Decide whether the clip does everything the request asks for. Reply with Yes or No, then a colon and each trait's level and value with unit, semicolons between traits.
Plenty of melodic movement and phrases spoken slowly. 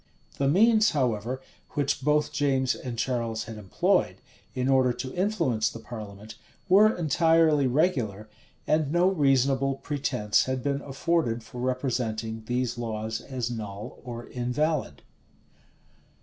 No: average, 4.4 semitones; slow, 125 wpm